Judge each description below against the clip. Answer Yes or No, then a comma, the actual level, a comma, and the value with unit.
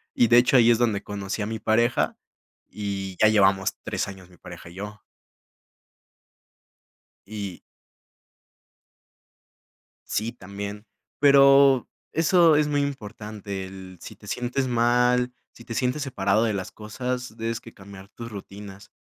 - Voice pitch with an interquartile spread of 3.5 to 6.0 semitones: Yes, average, 3.8 semitones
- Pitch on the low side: Yes, low, 110 Hz